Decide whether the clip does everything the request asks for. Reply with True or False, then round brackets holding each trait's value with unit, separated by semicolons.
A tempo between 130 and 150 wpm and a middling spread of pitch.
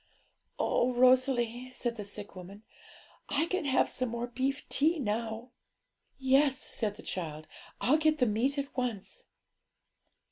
True (140 wpm; 3.9 semitones)